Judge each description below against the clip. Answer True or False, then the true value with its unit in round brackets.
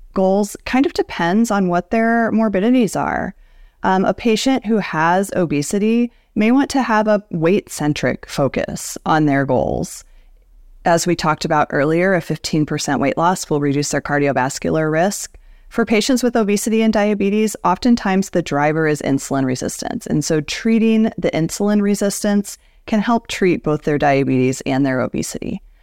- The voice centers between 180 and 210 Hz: True (185 Hz)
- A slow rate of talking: False (155 wpm)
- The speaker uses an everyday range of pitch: False (6.6 semitones)